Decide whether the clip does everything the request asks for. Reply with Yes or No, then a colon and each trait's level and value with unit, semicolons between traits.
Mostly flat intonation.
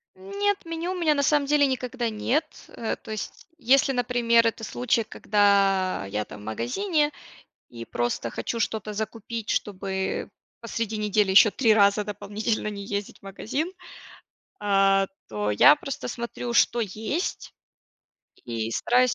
No: average, 4.2 semitones